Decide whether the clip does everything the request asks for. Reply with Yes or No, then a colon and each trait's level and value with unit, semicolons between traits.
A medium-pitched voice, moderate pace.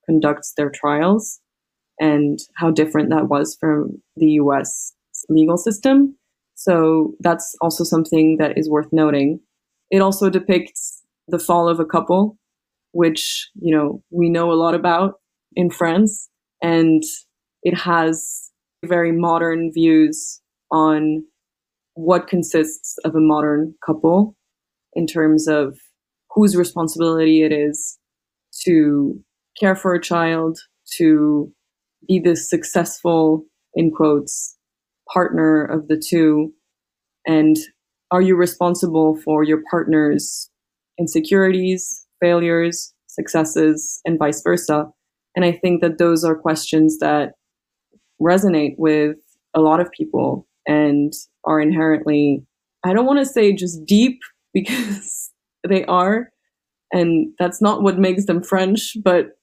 No: medium, 170 Hz; slow, 125 wpm